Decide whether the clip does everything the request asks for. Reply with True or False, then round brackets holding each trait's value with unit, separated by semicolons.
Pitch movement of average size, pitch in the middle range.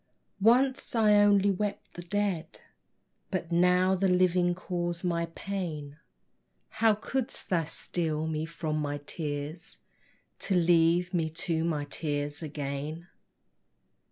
True (3.2 semitones; 175 Hz)